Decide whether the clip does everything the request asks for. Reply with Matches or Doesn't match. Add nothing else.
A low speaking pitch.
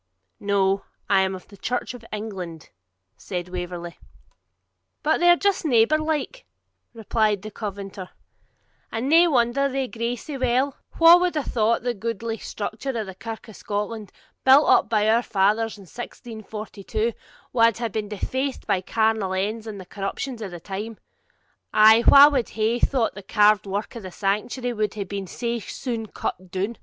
Doesn't match